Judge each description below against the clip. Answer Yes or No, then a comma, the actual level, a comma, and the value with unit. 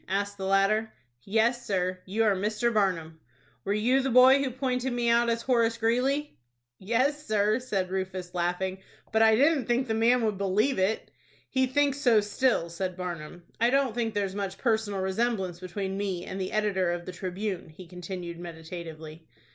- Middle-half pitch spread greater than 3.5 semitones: Yes, average, 4.3 semitones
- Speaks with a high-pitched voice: Yes, high, 205 Hz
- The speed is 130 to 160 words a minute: No, average, 180 wpm